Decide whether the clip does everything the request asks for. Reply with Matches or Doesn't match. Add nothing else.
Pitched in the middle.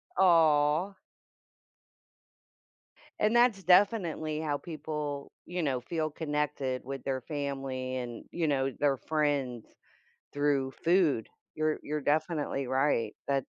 Matches